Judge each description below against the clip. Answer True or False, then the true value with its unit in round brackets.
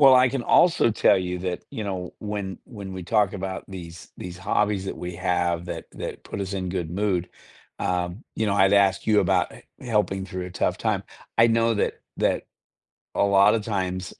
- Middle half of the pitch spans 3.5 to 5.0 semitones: False (2.6 semitones)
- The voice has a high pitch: False (95 Hz)